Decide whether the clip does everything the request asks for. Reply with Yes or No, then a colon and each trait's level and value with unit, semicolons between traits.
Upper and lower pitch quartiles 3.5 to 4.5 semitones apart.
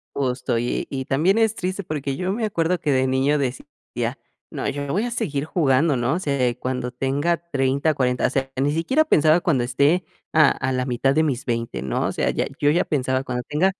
Yes: average, 4.0 semitones